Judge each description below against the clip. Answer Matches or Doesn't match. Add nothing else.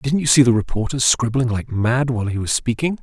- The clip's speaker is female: Doesn't match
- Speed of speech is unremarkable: Doesn't match